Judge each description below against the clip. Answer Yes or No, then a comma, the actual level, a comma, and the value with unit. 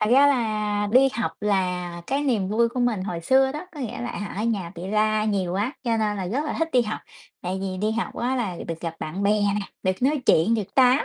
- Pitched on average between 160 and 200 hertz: No, high, 215 Hz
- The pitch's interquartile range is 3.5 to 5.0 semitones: Yes, average, 4.3 semitones